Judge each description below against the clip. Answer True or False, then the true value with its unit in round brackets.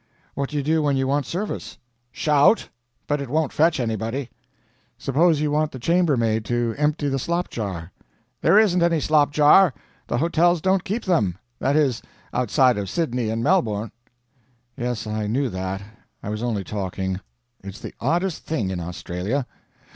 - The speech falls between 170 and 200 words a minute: False (160 wpm)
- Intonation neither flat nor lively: False (6.3 semitones)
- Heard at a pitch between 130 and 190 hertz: True (135 Hz)